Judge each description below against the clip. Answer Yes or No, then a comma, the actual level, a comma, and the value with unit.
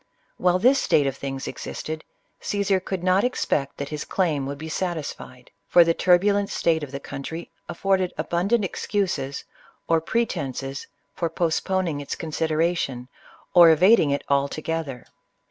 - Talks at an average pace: Yes, average, 145 wpm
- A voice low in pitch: No, medium, 165 Hz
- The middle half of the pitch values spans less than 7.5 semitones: Yes, average, 4.6 semitones